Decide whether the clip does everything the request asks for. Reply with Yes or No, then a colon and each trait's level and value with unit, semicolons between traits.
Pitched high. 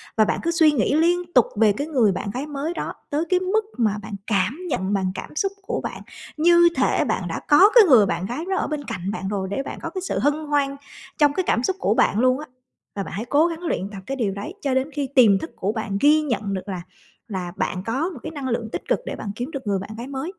Yes: very high, 265 Hz